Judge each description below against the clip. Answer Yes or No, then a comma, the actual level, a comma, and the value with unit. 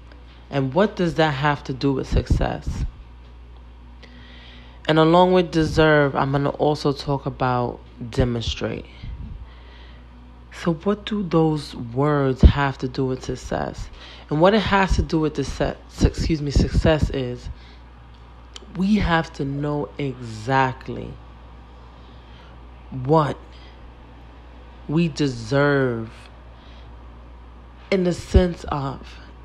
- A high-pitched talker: No, low, 120 Hz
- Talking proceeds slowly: Yes, slow, 110 wpm